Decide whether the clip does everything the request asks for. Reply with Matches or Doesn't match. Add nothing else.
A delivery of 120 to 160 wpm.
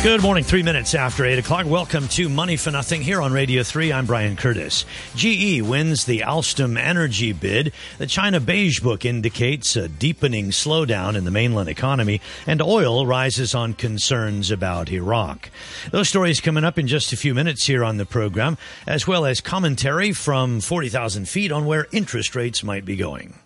Doesn't match